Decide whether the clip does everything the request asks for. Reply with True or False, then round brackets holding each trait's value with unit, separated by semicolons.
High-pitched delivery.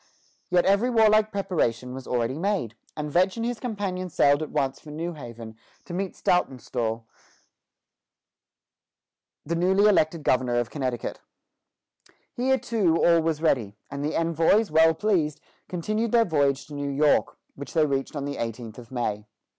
False (155 Hz)